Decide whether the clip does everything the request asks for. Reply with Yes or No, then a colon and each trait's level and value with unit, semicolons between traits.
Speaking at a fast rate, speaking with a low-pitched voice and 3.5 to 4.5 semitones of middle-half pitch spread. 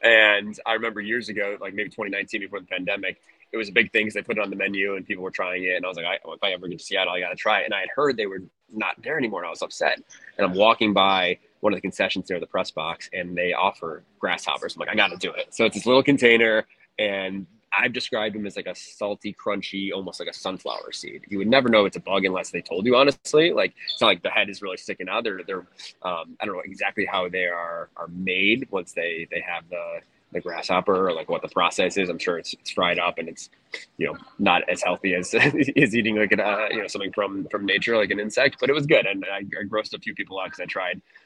No: fast, 275 wpm; low, 105 Hz; average, 2.9 semitones